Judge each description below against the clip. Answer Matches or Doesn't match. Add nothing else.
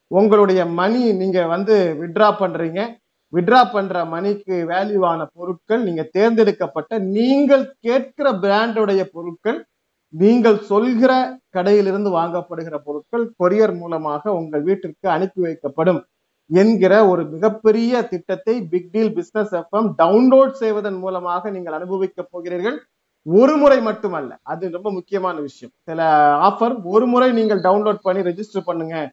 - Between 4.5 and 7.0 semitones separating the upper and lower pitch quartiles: Doesn't match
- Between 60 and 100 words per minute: Doesn't match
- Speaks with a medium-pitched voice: Doesn't match